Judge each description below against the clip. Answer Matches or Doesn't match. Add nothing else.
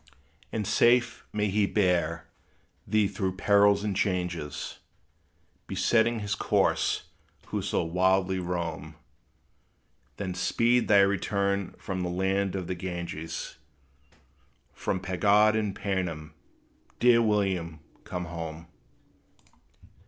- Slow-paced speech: Matches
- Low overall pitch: Matches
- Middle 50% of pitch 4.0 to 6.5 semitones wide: Doesn't match